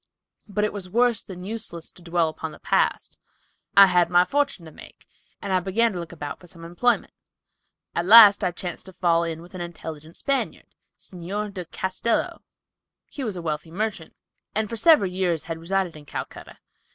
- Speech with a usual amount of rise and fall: Yes, average, 3.6 semitones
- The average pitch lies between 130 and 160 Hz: No, medium, 180 Hz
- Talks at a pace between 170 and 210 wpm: Yes, average, 190 wpm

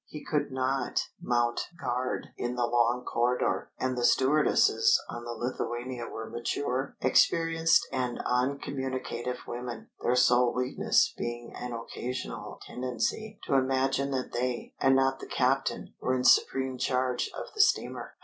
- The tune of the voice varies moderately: No, narrow, 1.7 semitones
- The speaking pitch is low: Yes, low, 125 Hz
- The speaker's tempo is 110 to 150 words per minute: Yes, average, 140 wpm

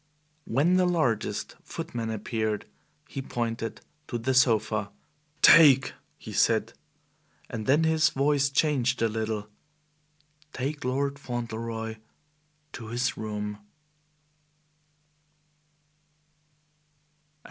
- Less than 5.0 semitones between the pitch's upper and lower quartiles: Yes, average, 3.9 semitones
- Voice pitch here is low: Yes, low, 120 Hz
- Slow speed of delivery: Yes, slow, 90 wpm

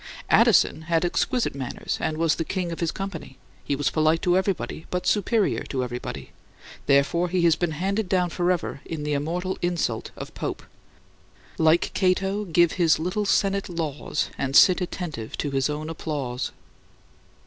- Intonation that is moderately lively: Yes, average, 3.5 semitones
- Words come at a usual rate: Yes, average, 160 wpm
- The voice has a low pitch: No, medium, 170 Hz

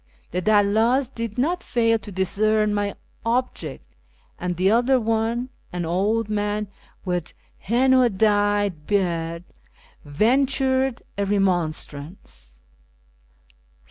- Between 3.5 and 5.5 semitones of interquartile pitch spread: Yes, average, 4.5 semitones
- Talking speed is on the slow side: Yes, slow, 110 wpm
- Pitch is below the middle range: No, high, 205 Hz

